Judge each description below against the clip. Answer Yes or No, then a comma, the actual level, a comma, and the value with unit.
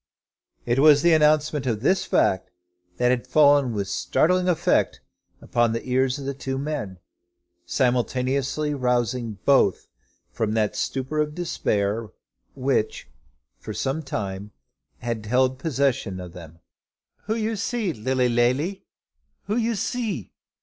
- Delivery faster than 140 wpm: No, slow, 135 wpm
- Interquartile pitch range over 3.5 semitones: Yes, average, 4.7 semitones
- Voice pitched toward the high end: No, low, 130 Hz